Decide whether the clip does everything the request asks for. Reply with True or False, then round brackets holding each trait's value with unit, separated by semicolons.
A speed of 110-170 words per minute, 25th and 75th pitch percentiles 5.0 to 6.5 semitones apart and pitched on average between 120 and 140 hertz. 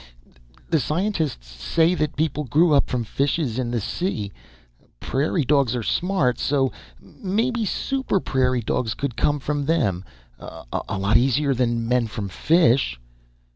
True (140 wpm; 5.4 semitones; 135 Hz)